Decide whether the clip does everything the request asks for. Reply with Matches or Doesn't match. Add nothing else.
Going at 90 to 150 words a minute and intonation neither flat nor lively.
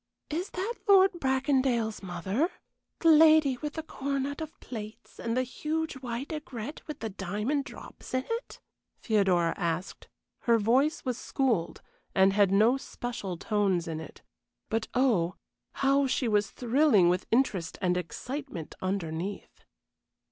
Doesn't match